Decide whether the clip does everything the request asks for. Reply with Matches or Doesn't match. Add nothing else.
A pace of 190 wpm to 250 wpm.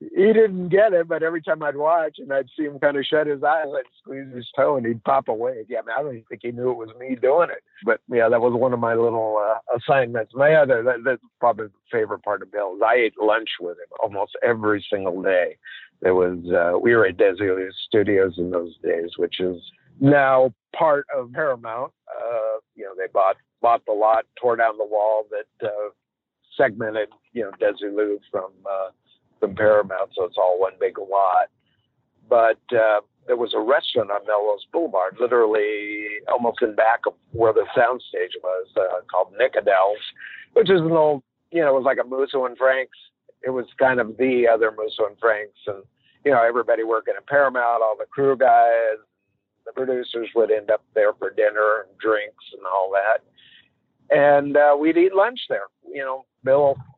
Matches